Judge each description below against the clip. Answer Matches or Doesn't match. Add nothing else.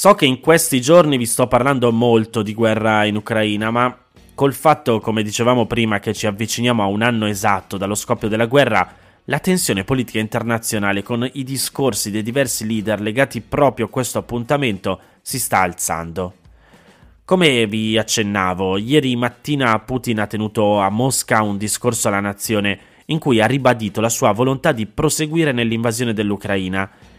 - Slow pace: Doesn't match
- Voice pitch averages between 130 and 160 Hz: Doesn't match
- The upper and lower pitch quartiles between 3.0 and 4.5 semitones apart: Matches